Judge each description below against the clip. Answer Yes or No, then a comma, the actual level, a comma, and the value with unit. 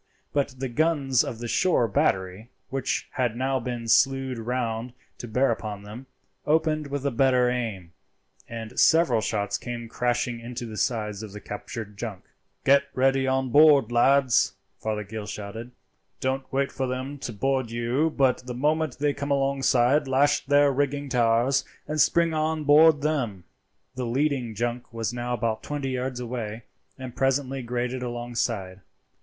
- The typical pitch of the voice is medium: No, low, 125 Hz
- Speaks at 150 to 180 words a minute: Yes, average, 160 wpm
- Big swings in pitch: No, average, 3.1 semitones